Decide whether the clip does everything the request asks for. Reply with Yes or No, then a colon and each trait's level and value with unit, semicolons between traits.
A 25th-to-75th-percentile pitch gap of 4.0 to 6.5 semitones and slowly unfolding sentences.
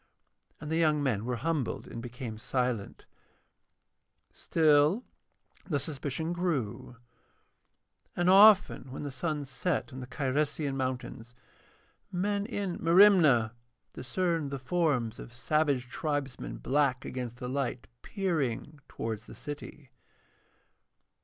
Yes: average, 4.7 semitones; slow, 115 wpm